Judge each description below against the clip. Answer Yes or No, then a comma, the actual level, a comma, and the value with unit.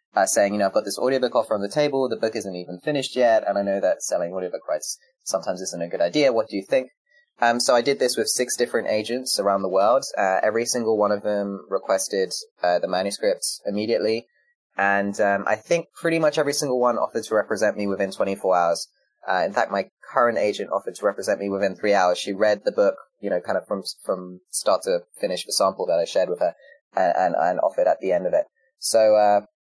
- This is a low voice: Yes, low, 120 Hz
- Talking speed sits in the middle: No, fast, 235 wpm